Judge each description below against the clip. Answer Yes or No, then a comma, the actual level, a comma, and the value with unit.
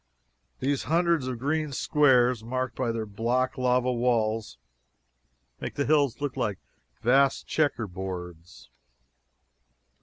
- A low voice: Yes, low, 125 Hz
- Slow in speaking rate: Yes, slow, 110 wpm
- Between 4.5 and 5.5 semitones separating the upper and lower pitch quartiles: No, average, 3.5 semitones